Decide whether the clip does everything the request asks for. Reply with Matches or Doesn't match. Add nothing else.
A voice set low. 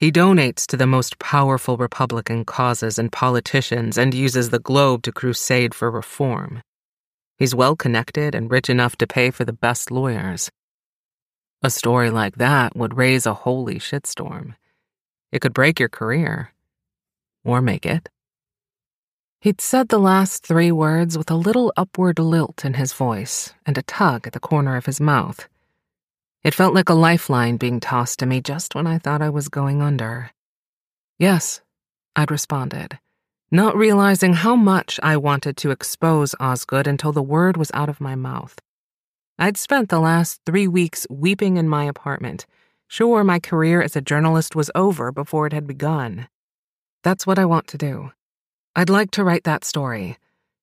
Doesn't match